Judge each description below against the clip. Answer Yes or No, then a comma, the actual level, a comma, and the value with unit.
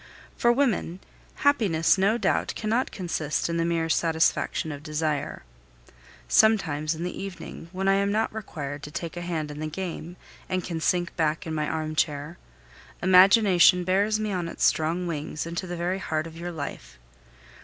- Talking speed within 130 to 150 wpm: No, average, 170 wpm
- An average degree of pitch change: Yes, average, 3.4 semitones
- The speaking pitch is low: No, medium, 170 Hz